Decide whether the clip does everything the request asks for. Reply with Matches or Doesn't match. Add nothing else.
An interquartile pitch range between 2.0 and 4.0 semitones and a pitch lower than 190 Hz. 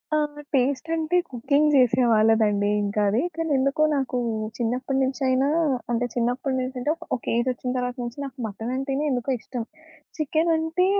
Doesn't match